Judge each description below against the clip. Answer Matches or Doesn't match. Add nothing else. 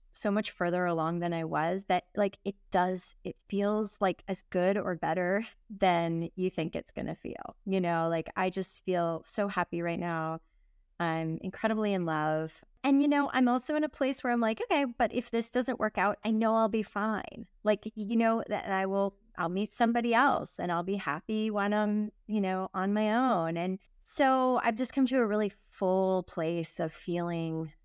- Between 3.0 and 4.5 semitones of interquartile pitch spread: Matches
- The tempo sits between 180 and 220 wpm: Matches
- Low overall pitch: Doesn't match